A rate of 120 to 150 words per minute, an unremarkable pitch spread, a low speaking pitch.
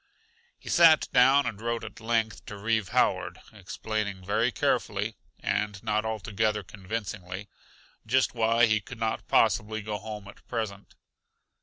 No: average, 140 wpm; narrow, 1.8 semitones; low, 110 Hz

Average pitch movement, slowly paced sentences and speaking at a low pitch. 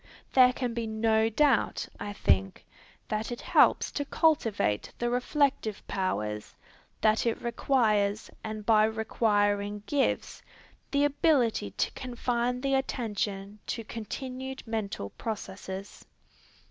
No: average, 3.5 semitones; slow, 115 wpm; high, 225 Hz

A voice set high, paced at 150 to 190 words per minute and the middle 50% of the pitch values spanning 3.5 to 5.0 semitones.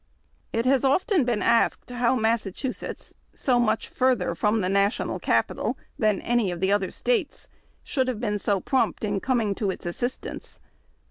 Yes: high, 230 Hz; average, 165 wpm; average, 4.0 semitones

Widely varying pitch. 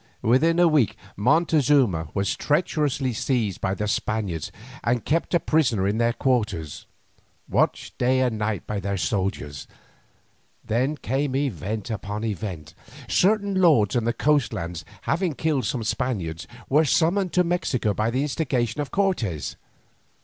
Yes: wide, 6.5 semitones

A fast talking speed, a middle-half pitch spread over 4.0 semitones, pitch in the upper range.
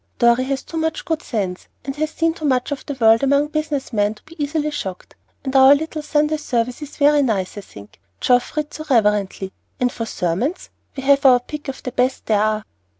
Yes: fast, 215 wpm; average, 4.9 semitones; very high, 265 Hz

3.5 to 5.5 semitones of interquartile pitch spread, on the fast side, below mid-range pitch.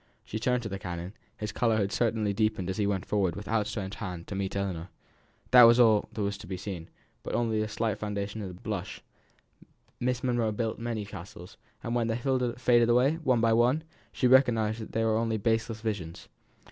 No: average, 2.8 semitones; fast, 210 wpm; low, 110 Hz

